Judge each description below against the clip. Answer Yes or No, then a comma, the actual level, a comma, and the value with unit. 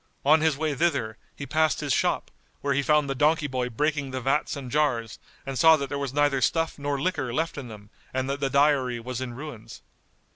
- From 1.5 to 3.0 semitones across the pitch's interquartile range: Yes, average, 2.7 semitones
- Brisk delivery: Yes, fast, 220 wpm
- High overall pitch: No, medium, 140 Hz